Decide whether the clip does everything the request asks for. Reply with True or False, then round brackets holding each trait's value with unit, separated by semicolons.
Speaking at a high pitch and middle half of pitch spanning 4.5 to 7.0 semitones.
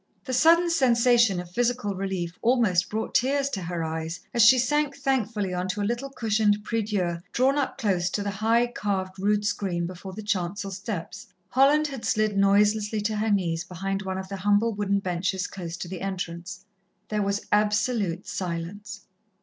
False (205 Hz; 3.7 semitones)